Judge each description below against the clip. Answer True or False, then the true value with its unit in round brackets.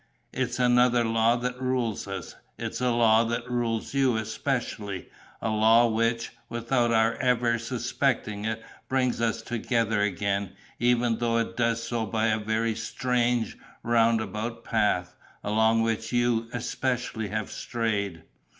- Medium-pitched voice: False (115 Hz)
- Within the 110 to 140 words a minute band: True (135 wpm)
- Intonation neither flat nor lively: False (1.6 semitones)